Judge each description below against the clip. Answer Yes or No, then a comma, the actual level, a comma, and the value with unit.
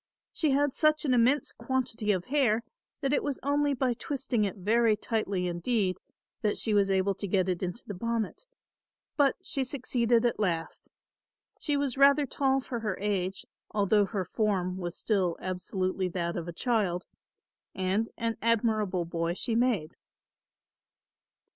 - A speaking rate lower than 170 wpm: Yes, average, 155 wpm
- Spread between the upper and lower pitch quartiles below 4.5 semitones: No, wide, 5.4 semitones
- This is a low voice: No, high, 215 Hz